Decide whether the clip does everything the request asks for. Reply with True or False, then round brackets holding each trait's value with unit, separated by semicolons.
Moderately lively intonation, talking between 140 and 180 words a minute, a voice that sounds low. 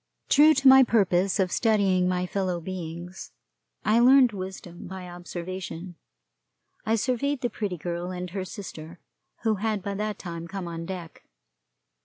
False (3.6 semitones; 150 wpm; 190 Hz)